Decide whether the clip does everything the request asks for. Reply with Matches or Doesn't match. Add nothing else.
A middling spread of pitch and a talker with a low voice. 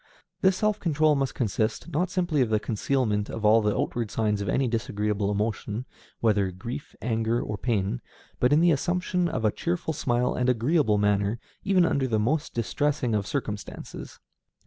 Doesn't match